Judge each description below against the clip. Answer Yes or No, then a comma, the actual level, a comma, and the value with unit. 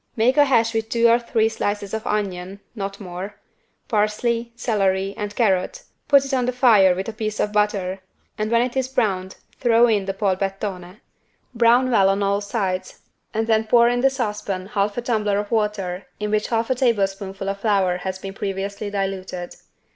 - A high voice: Yes, high, 210 Hz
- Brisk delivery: No, average, 185 wpm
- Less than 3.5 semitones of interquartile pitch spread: Yes, average, 3.1 semitones